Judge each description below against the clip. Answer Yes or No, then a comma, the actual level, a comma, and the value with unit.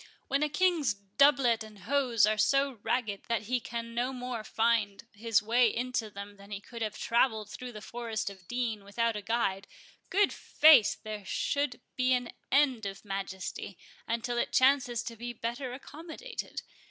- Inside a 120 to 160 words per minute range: No, average, 170 wpm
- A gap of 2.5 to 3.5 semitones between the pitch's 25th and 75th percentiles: Yes, average, 3.1 semitones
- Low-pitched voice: No, high, 235 Hz